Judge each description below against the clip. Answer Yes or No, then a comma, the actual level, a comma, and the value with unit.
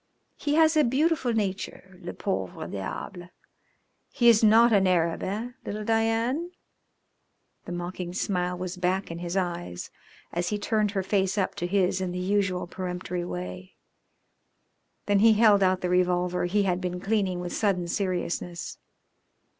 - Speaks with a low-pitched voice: No, medium, 185 Hz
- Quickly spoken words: No, average, 155 wpm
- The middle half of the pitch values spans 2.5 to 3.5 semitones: Yes, average, 3.0 semitones